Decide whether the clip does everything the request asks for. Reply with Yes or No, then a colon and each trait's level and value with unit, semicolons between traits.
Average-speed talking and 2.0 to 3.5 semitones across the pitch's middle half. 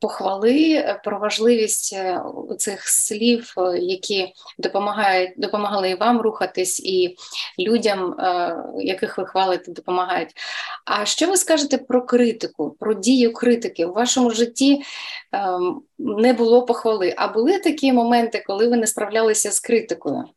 No: average, 125 wpm; average, 4.3 semitones